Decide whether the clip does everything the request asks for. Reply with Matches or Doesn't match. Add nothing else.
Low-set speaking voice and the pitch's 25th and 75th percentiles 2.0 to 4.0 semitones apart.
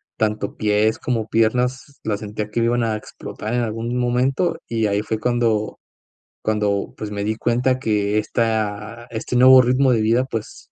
Matches